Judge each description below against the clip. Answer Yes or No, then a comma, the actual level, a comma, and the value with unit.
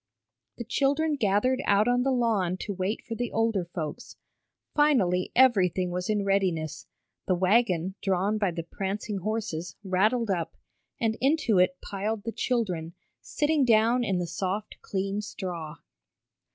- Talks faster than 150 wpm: No, average, 145 wpm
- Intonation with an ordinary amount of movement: Yes, average, 4.2 semitones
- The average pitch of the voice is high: Yes, high, 200 Hz